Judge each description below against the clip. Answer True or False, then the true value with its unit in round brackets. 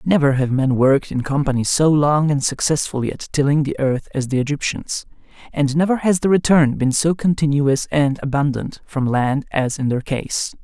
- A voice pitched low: False (145 Hz)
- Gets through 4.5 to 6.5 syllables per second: True (5.0 syllables/s)